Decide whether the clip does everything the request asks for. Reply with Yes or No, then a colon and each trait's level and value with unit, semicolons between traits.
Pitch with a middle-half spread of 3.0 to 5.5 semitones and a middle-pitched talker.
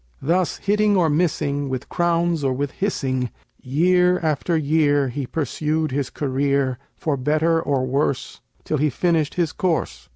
Yes: average, 3.4 semitones; medium, 150 Hz